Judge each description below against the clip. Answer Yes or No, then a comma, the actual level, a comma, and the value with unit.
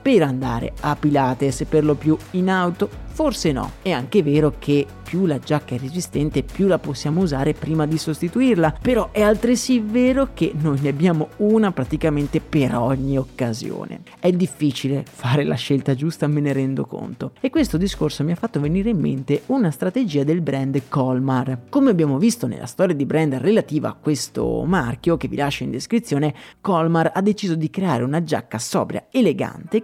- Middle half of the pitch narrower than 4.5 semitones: No, average, 5.2 semitones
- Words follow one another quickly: Yes, fast, 180 wpm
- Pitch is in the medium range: Yes, medium, 155 Hz